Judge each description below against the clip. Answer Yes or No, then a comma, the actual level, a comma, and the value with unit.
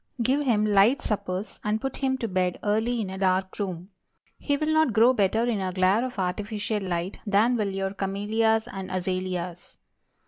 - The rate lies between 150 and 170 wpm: No, average, 180 wpm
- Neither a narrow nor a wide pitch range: Yes, average, 3.4 semitones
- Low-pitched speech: No, high, 205 Hz